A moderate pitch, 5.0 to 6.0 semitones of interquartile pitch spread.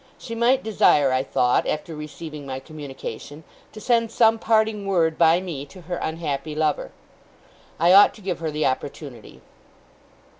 Yes: medium, 160 Hz; wide, 5.6 semitones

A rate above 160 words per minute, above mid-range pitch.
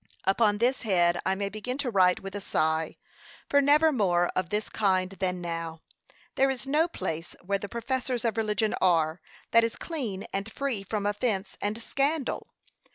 Yes: average, 175 wpm; high, 205 Hz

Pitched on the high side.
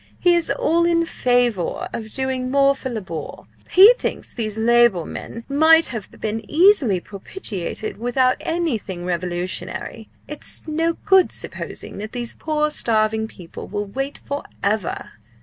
Yes: high, 240 Hz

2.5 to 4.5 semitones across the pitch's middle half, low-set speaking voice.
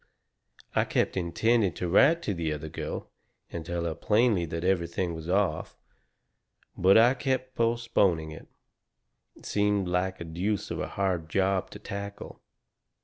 Yes: average, 3.7 semitones; very low, 95 Hz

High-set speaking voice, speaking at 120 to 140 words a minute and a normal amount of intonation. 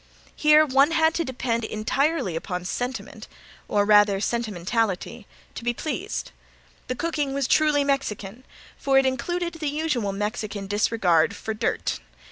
No: high, 240 Hz; slow, 135 wpm; wide, 6.1 semitones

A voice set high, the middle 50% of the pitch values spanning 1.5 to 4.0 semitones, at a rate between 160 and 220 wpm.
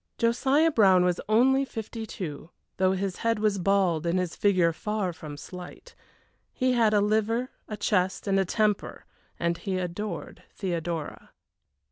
No: high, 200 Hz; average, 3.7 semitones; average, 150 wpm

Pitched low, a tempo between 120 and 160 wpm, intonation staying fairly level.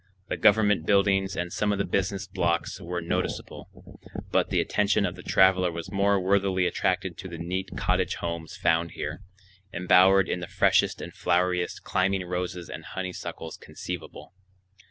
Yes: very low, 90 Hz; average, 155 wpm; narrow, 1.7 semitones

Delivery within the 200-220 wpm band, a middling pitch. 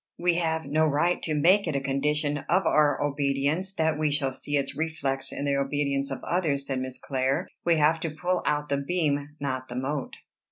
Yes: fast, 205 wpm; medium, 145 Hz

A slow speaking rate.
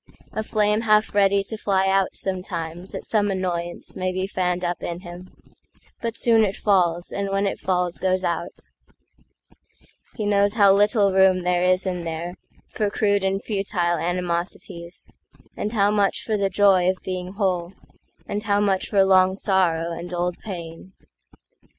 No: average, 145 wpm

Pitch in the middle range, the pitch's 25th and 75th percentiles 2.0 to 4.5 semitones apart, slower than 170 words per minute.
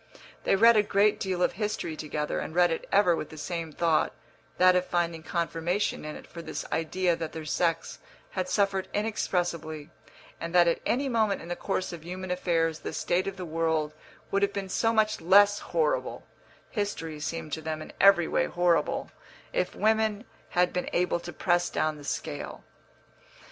No: medium, 175 Hz; average, 3.4 semitones; average, 185 wpm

